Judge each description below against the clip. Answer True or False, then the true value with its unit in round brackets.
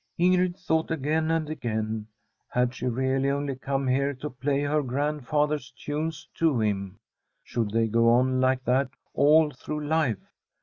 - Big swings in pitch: False (3.5 semitones)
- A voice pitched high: False (140 Hz)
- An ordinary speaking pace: True (150 wpm)